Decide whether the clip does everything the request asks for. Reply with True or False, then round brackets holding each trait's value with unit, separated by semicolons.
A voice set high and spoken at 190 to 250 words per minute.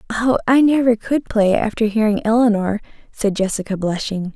False (220 Hz; 150 wpm)